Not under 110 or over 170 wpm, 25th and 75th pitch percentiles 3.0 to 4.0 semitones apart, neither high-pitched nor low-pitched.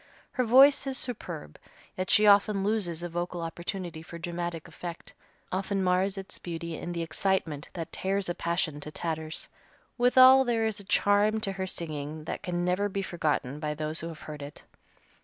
No: average, 180 wpm; average, 3.6 semitones; medium, 175 Hz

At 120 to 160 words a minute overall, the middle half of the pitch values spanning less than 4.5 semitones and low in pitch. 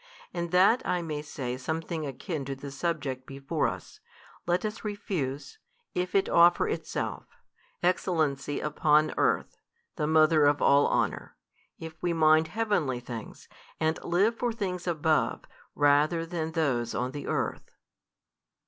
No: average, 140 wpm; average, 3.6 semitones; medium, 160 Hz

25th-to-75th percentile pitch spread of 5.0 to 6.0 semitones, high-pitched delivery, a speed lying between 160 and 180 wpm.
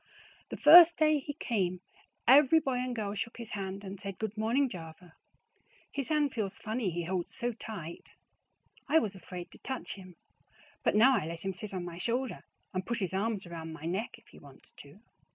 No: wide, 5.5 semitones; high, 210 Hz; average, 200 wpm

